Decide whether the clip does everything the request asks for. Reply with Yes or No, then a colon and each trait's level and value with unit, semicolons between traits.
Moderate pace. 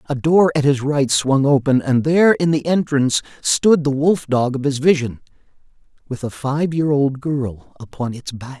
Yes: average, 195 wpm